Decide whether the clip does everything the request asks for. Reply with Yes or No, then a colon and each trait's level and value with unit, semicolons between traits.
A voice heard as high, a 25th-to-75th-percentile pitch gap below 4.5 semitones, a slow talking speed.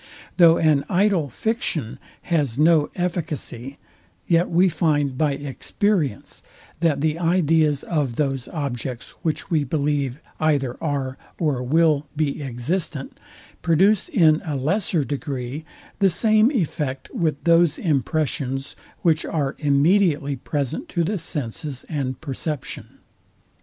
No: medium, 150 Hz; average, 3.4 semitones; slow, 120 wpm